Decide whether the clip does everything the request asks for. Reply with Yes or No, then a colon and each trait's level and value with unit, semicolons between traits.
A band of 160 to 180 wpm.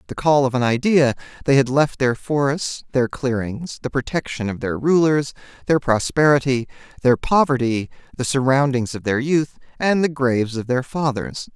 Yes: average, 170 wpm